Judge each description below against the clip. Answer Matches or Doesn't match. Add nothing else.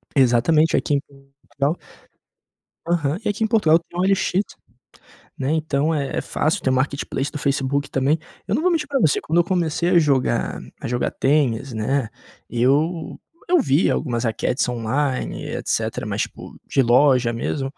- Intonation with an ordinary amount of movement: Matches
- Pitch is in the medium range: Matches